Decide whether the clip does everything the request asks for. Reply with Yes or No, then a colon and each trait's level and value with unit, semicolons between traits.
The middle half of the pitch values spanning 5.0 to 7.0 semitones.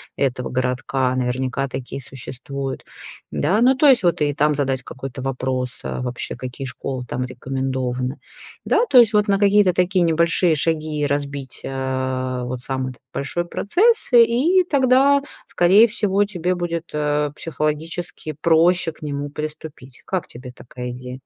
Yes: wide, 5.6 semitones